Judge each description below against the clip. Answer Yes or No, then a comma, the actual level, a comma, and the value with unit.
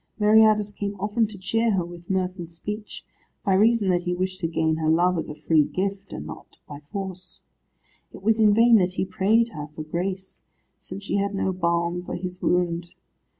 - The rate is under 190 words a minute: No, average, 200 wpm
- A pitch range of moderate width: Yes, average, 3.1 semitones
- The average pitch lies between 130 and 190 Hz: Yes, medium, 185 Hz